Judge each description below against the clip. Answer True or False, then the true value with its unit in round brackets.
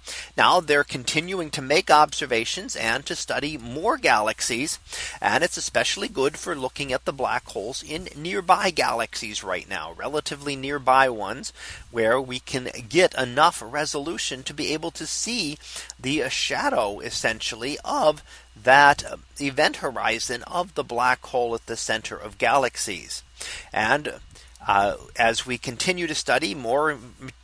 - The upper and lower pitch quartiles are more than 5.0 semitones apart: False (3.1 semitones)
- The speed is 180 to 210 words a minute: False (140 wpm)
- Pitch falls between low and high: True (145 Hz)